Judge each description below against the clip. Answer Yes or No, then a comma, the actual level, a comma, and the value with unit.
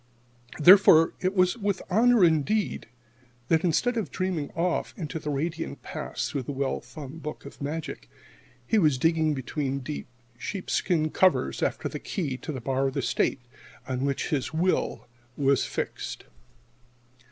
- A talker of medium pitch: Yes, medium, 155 Hz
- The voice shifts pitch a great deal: No, average, 4.8 semitones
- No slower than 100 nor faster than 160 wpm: Yes, average, 150 wpm